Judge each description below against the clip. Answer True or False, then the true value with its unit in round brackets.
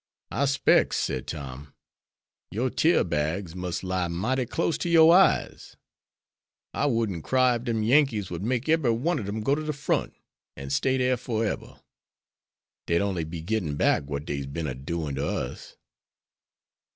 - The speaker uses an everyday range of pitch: False (8.2 semitones)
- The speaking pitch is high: False (105 Hz)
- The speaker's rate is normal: True (165 wpm)